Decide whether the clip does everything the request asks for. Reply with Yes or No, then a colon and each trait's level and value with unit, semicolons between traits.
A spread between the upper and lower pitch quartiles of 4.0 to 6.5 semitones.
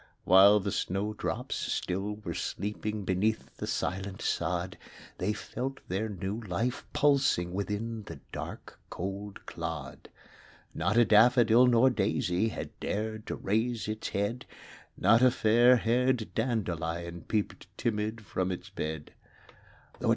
No: average, 3.2 semitones